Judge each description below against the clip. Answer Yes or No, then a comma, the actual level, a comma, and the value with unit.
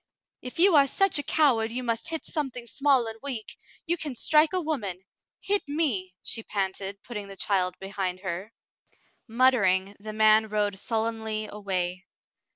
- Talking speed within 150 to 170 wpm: Yes, average, 160 wpm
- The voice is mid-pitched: No, high, 220 Hz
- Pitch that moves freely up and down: Yes, wide, 5.8 semitones